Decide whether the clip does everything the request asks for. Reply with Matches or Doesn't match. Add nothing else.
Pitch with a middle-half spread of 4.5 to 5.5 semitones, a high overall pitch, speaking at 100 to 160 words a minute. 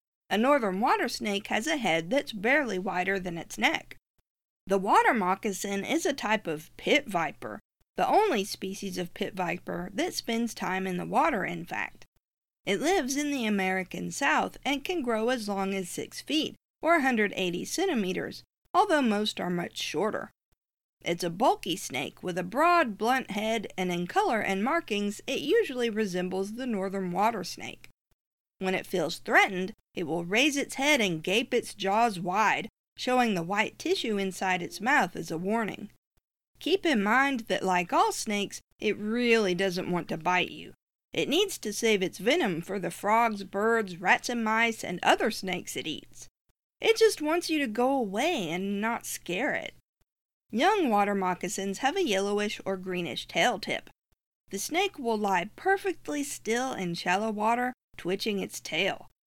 Doesn't match